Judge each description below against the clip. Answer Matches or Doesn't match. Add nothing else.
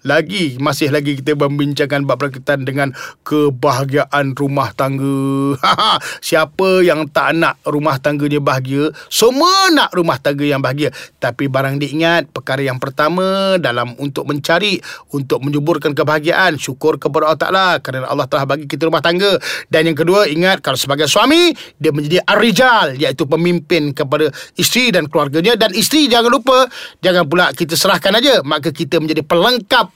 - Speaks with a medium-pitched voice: Matches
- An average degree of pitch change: Matches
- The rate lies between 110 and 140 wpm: Doesn't match